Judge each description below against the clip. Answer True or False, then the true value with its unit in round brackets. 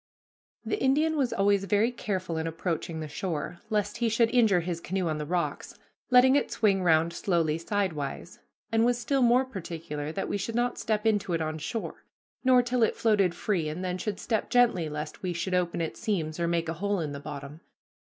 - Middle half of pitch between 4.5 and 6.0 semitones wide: True (5.5 semitones)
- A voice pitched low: False (185 Hz)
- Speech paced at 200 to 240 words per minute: True (205 wpm)